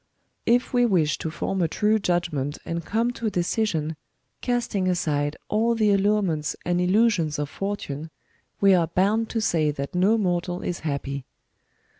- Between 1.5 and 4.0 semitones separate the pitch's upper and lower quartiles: No, average, 5.2 semitones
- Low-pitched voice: No, medium, 180 Hz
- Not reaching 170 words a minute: Yes, average, 160 wpm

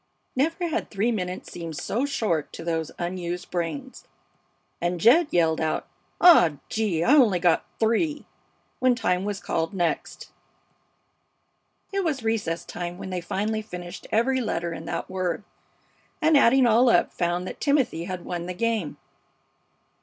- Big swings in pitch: Yes, wide, 5.9 semitones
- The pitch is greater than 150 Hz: Yes, high, 190 Hz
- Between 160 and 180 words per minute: No, average, 150 wpm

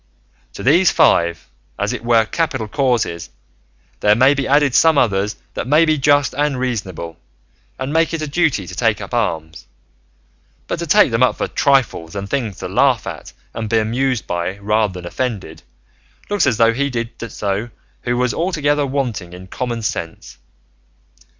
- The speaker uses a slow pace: No, average, 170 wpm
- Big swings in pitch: Yes, wide, 6.0 semitones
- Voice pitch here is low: Yes, low, 120 Hz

